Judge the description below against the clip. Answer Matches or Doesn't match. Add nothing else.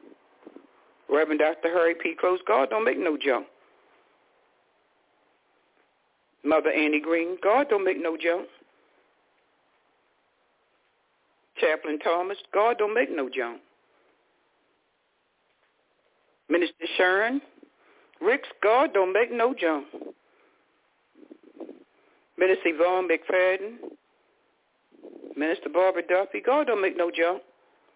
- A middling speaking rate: Doesn't match